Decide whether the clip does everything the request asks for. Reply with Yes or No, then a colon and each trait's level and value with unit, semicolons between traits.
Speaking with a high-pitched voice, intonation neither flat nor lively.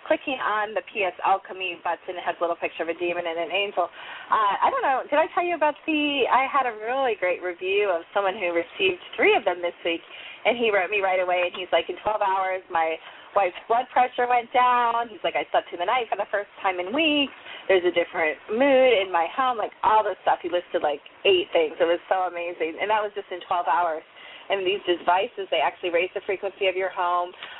No: high, 195 Hz; wide, 6.3 semitones